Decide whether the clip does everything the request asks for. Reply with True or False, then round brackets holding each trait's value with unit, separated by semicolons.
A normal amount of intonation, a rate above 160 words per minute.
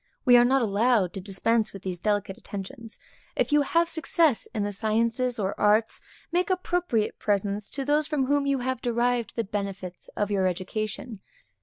True (4.7 semitones; 175 wpm)